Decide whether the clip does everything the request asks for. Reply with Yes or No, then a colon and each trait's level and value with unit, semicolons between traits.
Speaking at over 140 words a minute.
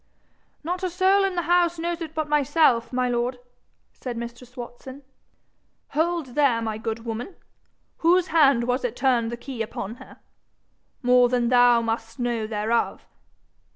Yes: average, 155 wpm